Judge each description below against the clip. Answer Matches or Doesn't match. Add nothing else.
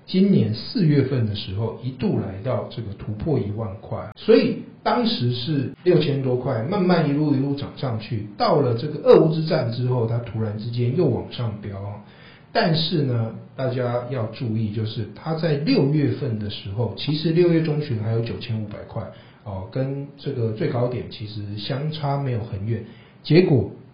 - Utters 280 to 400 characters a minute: Doesn't match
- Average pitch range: Matches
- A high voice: Doesn't match